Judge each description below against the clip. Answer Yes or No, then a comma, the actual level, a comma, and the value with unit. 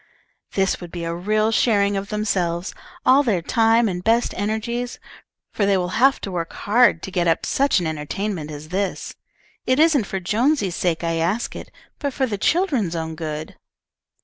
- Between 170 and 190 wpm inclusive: Yes, average, 180 wpm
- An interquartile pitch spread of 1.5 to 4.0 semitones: No, average, 5.2 semitones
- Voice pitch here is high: Yes, high, 200 Hz